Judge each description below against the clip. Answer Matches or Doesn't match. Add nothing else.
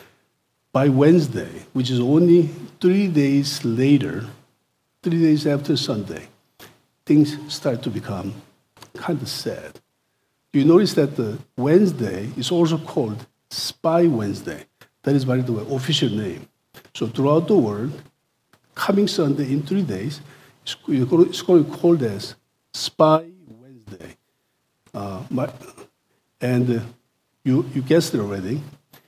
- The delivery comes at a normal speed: Doesn't match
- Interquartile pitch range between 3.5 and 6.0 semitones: Matches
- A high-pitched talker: Doesn't match